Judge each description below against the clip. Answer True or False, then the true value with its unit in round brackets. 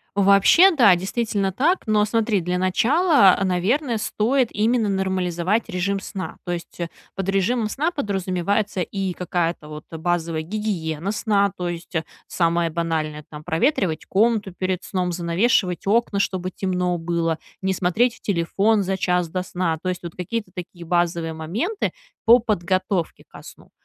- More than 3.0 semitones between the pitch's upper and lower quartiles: True (3.6 semitones)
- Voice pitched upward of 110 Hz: True (185 Hz)